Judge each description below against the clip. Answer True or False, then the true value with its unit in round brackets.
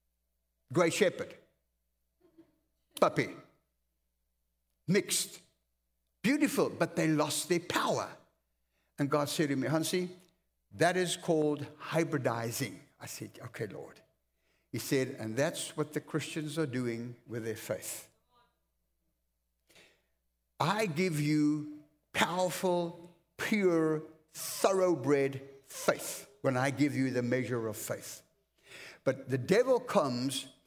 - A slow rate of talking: True (110 wpm)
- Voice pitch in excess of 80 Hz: True (135 Hz)